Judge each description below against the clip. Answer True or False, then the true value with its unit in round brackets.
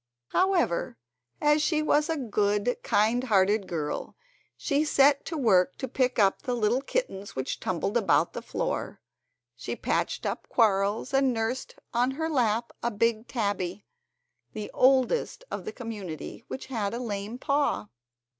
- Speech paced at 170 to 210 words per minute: False (145 wpm)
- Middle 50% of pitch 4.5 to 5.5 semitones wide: True (5.0 semitones)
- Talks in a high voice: True (235 Hz)